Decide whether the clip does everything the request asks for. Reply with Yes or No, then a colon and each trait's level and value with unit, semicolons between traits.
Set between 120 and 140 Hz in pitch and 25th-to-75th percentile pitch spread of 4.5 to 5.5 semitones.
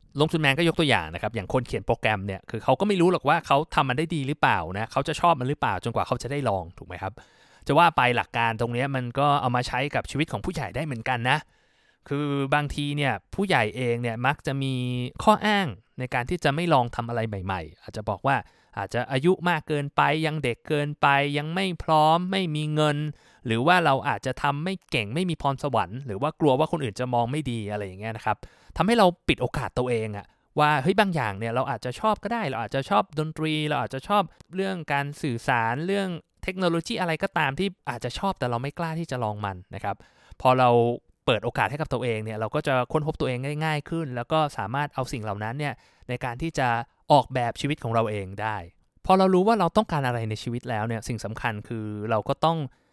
Yes: low, 135 Hz; average, 5.0 semitones